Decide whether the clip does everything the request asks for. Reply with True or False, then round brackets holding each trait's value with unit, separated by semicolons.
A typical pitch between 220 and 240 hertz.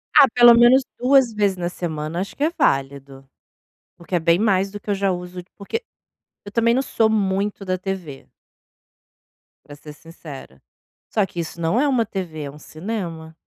False (185 Hz)